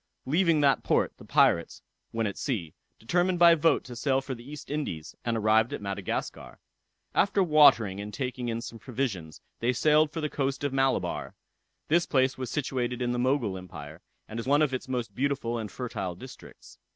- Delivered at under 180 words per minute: No, average, 190 wpm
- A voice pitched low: Yes, low, 130 Hz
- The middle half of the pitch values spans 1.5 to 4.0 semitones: No, average, 4.4 semitones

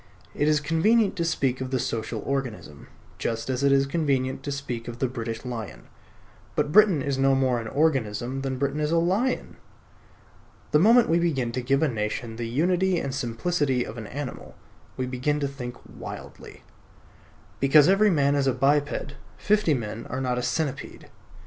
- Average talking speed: Yes, average, 180 wpm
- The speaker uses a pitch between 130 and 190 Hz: Yes, low, 135 Hz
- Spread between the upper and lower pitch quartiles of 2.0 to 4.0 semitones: Yes, average, 3.7 semitones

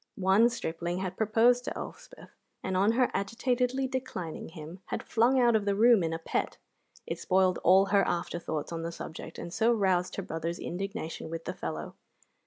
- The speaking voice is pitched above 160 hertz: Yes, high, 190 Hz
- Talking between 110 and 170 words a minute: No, average, 190 wpm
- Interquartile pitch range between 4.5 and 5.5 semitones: Yes, average, 5.1 semitones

